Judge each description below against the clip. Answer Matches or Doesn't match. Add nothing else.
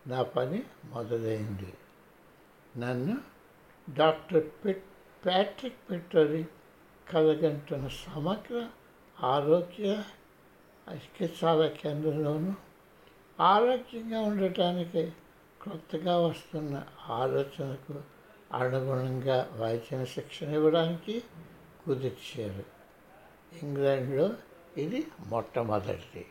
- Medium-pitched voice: Matches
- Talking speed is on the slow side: Matches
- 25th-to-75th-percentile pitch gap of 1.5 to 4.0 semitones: Doesn't match